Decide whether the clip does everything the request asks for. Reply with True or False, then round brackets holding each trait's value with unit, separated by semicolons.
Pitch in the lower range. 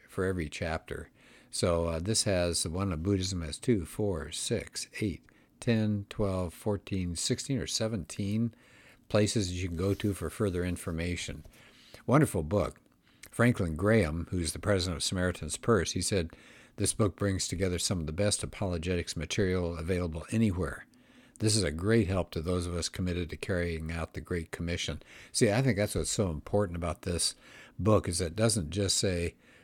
True (95 Hz)